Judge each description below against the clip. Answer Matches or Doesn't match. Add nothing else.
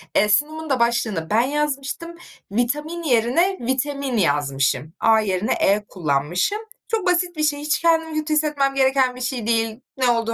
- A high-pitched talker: Matches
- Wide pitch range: Matches